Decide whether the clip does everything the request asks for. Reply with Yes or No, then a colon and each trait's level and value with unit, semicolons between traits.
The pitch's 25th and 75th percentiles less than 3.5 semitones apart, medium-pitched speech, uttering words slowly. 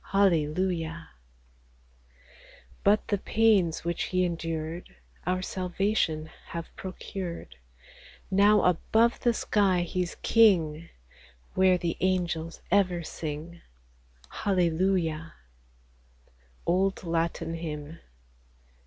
Yes: average, 2.7 semitones; medium, 175 Hz; slow, 85 wpm